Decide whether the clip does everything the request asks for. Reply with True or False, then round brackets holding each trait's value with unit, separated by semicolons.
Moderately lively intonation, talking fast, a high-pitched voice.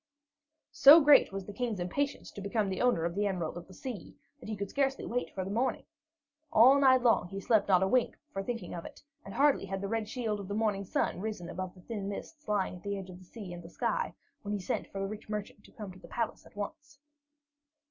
True (4.2 semitones; 250 wpm; 205 Hz)